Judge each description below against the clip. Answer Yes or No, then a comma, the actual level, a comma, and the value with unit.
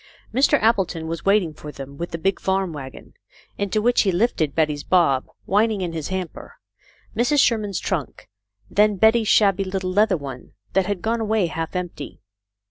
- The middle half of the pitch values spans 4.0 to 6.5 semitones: Yes, average, 4.6 semitones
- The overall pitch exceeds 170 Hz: Yes, high, 190 Hz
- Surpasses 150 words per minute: Yes, average, 180 wpm